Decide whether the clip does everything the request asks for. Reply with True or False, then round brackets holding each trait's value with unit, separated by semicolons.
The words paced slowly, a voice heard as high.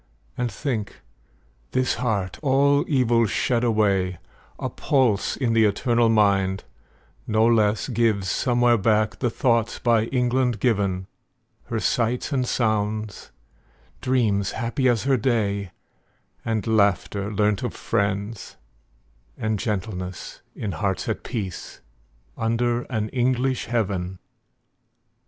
False (115 wpm; 110 Hz)